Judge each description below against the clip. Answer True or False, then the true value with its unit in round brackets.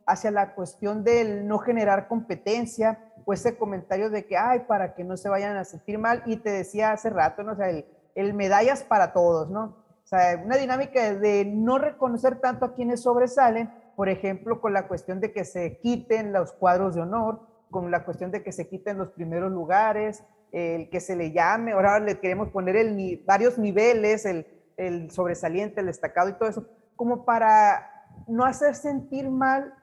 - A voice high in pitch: True (210 Hz)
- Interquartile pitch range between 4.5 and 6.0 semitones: False (3.8 semitones)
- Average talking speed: False (195 wpm)